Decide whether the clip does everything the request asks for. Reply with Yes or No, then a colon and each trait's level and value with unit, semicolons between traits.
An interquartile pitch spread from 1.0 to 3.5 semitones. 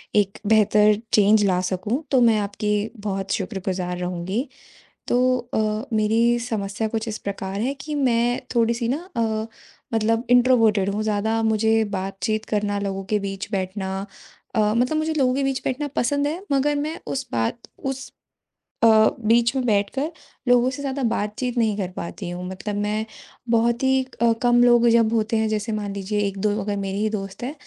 Yes: average, 3.1 semitones